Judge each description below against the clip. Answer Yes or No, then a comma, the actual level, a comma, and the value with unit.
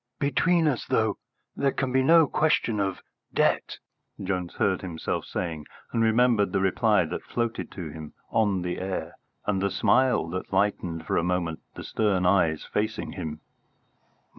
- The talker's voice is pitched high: No, low, 100 Hz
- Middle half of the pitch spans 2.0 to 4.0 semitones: No, average, 4.8 semitones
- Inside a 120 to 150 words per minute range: No, average, 160 wpm